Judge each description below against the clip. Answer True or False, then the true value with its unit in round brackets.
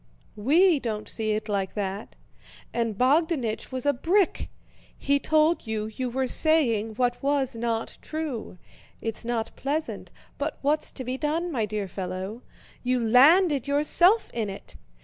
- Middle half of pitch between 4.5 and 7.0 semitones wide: True (5.5 semitones)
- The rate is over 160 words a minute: False (150 wpm)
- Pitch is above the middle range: True (250 Hz)